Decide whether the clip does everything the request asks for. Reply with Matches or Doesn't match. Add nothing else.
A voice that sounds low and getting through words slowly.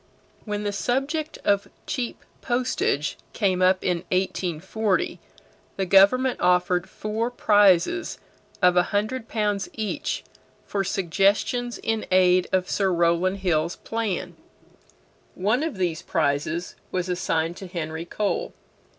Doesn't match